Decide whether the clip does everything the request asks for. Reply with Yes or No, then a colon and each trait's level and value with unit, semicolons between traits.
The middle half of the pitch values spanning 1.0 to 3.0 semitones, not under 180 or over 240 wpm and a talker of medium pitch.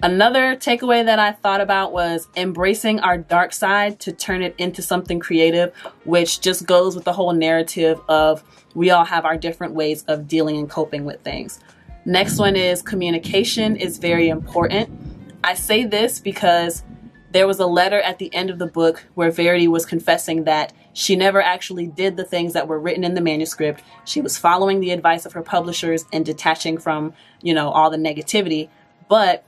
Yes: narrow, 2.6 semitones; average, 185 wpm; medium, 175 Hz